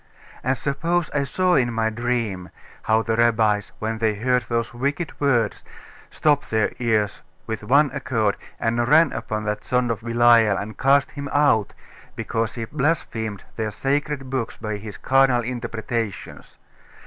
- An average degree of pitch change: Yes, average, 3.6 semitones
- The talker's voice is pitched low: Yes, low, 115 Hz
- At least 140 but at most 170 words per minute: Yes, average, 150 wpm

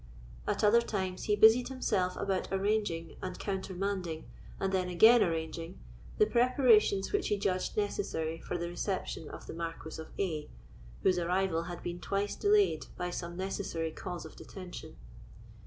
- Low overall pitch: No, high, 190 Hz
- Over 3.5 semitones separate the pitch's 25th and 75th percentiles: No, average, 3.1 semitones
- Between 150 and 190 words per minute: Yes, average, 155 wpm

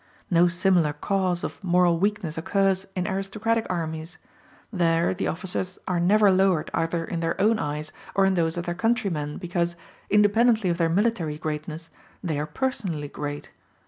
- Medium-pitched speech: Yes, medium, 180 Hz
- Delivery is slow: No, average, 160 wpm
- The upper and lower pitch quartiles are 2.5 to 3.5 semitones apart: Yes, average, 3.1 semitones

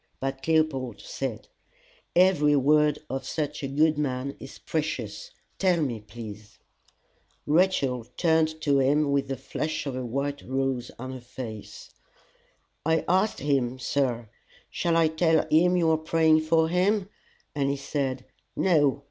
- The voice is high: No, medium, 145 Hz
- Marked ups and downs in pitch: No, average, 3.3 semitones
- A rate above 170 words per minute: No, average, 145 wpm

